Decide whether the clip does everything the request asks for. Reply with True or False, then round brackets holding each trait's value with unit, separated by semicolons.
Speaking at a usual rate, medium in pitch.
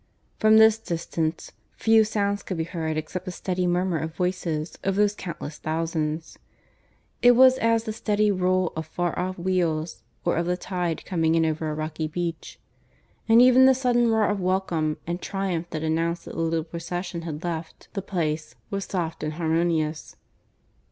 True (175 wpm; 175 Hz)